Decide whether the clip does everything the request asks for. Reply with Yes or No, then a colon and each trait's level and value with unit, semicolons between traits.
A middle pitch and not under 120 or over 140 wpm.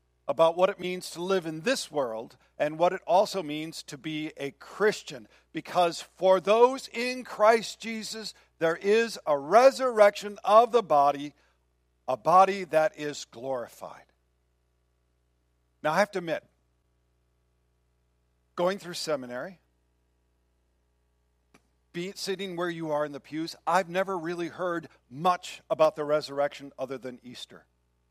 Yes: medium, 150 Hz; slow, 135 wpm